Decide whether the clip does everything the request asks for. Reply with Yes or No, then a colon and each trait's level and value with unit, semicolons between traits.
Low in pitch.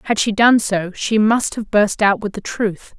No: high, 210 Hz